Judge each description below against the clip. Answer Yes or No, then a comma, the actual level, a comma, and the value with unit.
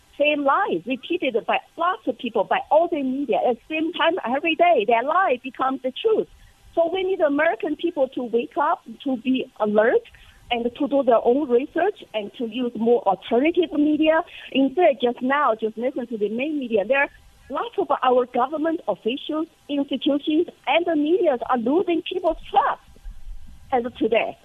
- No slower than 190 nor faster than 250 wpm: No, average, 175 wpm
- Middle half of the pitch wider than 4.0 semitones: Yes, average, 4.9 semitones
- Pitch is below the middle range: No, very high, 285 Hz